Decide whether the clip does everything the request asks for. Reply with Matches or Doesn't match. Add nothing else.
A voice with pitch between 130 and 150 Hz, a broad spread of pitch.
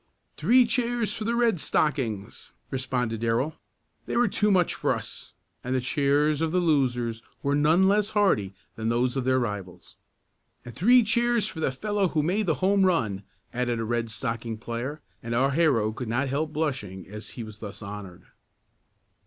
Matches